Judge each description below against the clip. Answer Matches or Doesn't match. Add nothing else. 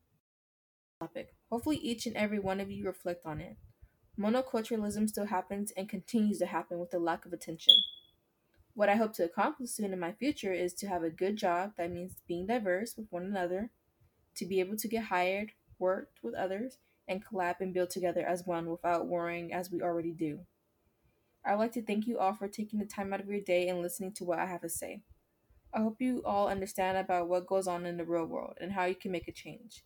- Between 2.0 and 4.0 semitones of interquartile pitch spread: Matches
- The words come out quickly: Matches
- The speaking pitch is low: Doesn't match